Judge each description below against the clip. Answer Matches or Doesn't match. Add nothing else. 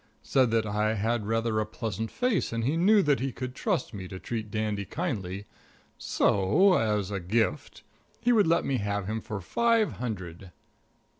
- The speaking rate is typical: Matches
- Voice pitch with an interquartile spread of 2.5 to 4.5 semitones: Doesn't match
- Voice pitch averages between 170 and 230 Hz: Doesn't match